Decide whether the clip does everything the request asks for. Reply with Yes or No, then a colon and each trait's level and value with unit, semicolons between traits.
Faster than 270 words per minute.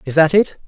No: fast, 265 wpm